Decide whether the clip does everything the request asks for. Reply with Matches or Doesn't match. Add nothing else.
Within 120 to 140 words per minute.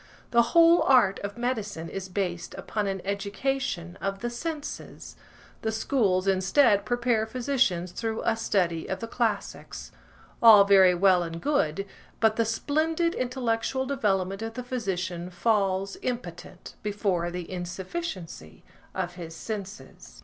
Matches